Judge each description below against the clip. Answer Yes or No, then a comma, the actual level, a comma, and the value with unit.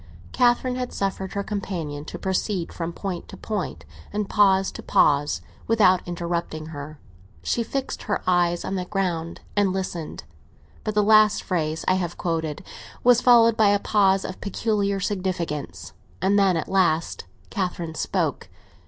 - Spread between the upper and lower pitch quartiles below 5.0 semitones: Yes, average, 3.4 semitones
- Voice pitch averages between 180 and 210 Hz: Yes, high, 190 Hz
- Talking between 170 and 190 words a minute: No, average, 155 wpm